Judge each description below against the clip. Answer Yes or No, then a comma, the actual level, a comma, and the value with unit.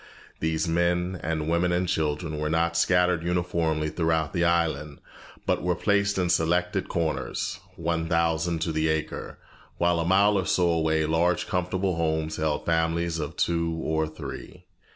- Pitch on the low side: Yes, very low, 85 Hz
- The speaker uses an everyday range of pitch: No, narrow, 1.8 semitones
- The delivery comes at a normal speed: Yes, average, 155 wpm